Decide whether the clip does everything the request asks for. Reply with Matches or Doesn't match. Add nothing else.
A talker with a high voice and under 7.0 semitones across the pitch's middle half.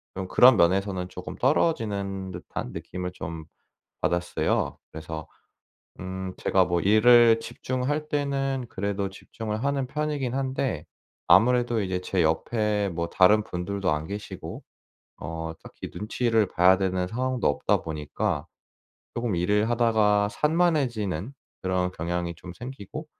Doesn't match